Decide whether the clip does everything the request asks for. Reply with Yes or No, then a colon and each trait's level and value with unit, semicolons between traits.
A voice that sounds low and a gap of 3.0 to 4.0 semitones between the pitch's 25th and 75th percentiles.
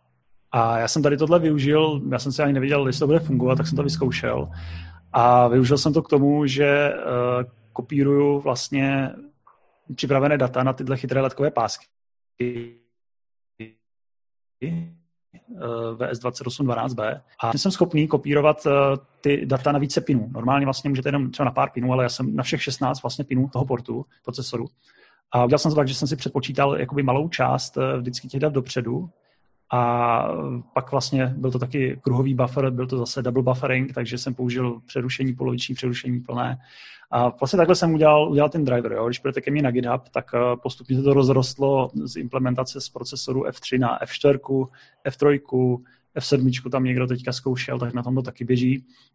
No: low, 130 Hz; narrow, 2.5 semitones